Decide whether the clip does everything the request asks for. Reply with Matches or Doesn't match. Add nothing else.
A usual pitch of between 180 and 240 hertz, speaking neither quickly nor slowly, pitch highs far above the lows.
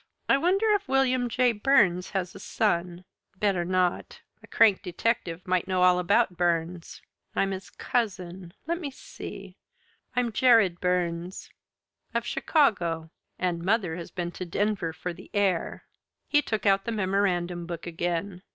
Doesn't match